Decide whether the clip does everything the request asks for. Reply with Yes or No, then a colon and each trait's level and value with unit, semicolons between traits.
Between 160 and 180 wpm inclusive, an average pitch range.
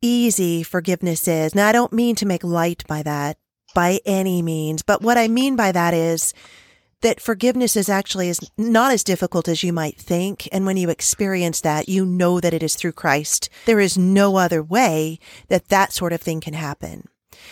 No: average, 200 wpm; average, 3.4 semitones